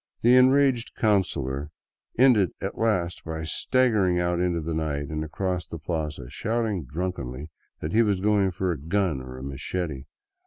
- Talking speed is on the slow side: No, average, 165 wpm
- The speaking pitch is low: Yes, very low, 90 Hz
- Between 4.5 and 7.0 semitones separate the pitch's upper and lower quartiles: Yes, average, 5.3 semitones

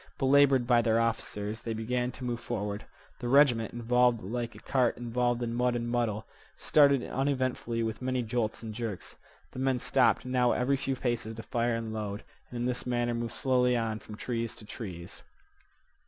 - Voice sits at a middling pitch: No, low, 120 Hz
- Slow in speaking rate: No, average, 185 wpm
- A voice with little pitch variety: Yes, narrow, 1.8 semitones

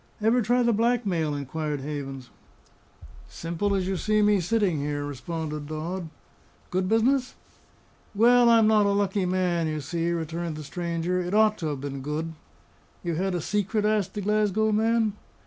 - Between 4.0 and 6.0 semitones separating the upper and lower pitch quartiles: Yes, average, 5.2 semitones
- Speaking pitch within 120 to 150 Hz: No, medium, 180 Hz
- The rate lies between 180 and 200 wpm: No, average, 165 wpm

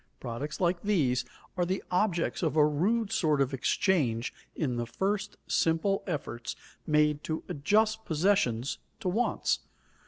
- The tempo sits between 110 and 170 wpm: Yes, slow, 135 wpm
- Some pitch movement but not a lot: No, wide, 5.7 semitones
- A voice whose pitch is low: No, medium, 165 Hz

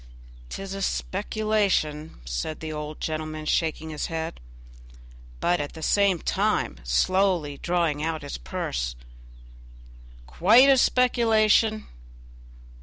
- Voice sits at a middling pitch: Yes, medium, 165 Hz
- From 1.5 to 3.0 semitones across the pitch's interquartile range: No, average, 4.8 semitones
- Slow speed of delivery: Yes, slow, 110 wpm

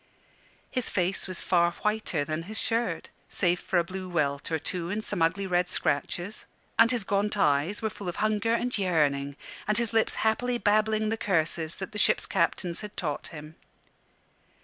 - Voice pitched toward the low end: No, high, 190 Hz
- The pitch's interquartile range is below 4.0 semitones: No, average, 4.4 semitones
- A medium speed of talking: Yes, average, 180 wpm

